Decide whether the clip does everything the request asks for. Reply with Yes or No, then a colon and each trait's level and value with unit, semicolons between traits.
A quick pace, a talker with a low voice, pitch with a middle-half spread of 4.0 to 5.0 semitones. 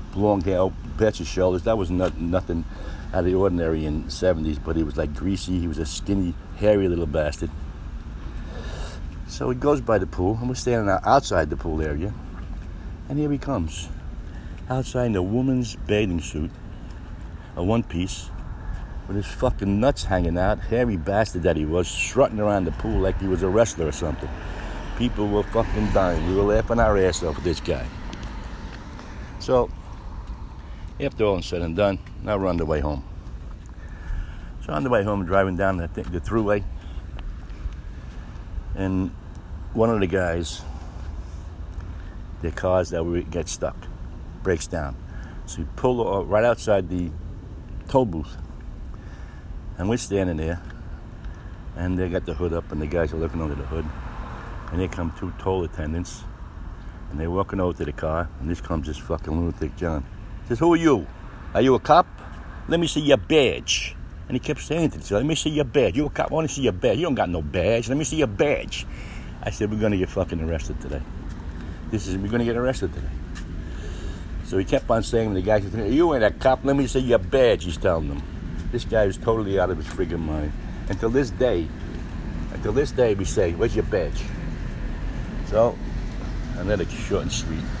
No: average, 190 wpm; very low, 90 Hz; average, 4.5 semitones